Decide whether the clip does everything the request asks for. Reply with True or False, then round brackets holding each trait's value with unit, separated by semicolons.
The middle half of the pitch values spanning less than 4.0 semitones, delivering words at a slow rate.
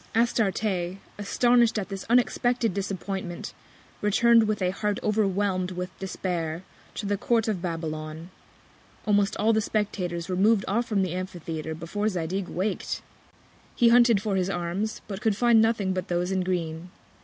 False (3.3 semitones; 155 wpm)